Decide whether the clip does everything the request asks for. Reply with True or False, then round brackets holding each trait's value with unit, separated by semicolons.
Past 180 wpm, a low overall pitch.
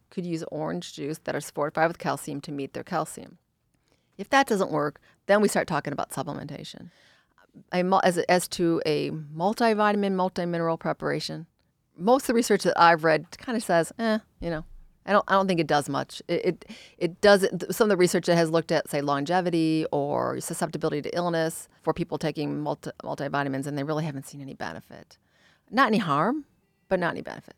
False (190 wpm; 170 Hz)